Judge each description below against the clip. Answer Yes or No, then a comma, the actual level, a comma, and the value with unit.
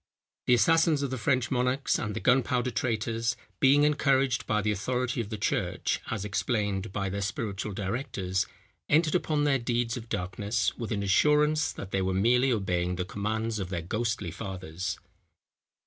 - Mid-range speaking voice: No, low, 115 Hz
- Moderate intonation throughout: Yes, average, 4.5 semitones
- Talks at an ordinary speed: Yes, average, 165 wpm